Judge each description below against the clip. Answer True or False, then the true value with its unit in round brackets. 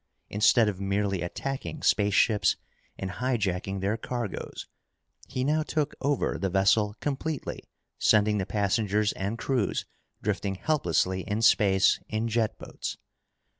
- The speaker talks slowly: True (125 wpm)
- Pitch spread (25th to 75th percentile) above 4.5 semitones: False (3.8 semitones)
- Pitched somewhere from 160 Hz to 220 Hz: False (105 Hz)